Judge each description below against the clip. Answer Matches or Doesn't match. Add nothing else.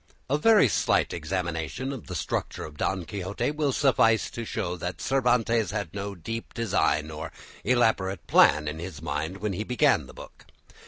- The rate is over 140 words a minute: Matches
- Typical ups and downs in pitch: Doesn't match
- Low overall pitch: Matches